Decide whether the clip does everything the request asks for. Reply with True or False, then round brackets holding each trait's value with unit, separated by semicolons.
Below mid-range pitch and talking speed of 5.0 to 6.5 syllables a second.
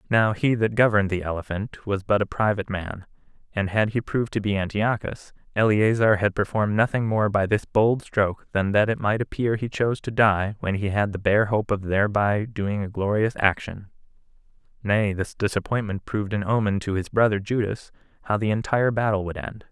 True (105 Hz; 5.5 syllables/s)